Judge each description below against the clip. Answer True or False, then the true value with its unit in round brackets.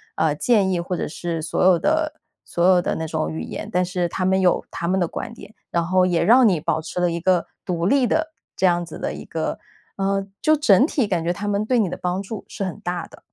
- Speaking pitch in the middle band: True (180 Hz)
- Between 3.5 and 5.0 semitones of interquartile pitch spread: False (2.9 semitones)